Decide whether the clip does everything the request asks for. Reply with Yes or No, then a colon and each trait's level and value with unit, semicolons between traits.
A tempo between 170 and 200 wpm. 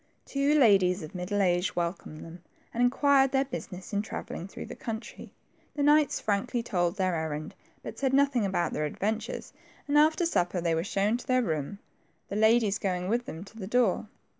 Yes: average, 190 wpm